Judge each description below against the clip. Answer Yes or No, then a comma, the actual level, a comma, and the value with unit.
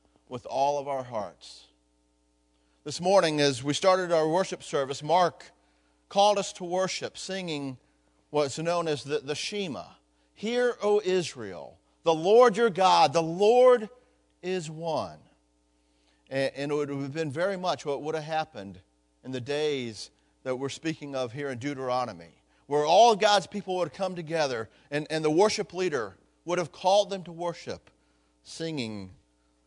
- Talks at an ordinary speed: Yes, average, 160 wpm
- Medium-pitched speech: Yes, medium, 150 Hz